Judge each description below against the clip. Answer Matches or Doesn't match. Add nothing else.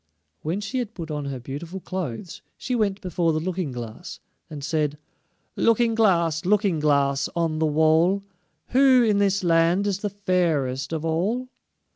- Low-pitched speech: Doesn't match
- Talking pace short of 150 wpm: Doesn't match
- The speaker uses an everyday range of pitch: Matches